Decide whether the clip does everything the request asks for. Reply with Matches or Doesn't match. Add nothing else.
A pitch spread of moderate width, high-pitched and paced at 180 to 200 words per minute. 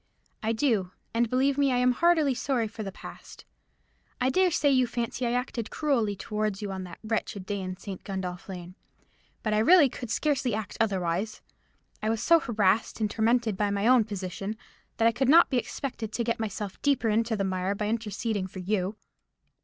Matches